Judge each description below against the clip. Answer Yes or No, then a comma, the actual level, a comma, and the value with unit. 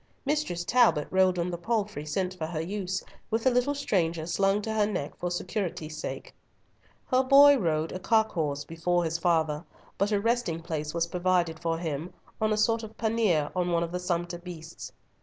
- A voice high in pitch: No, medium, 180 Hz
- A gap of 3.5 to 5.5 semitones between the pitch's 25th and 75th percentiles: Yes, average, 4.5 semitones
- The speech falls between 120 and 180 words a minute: No, average, 195 wpm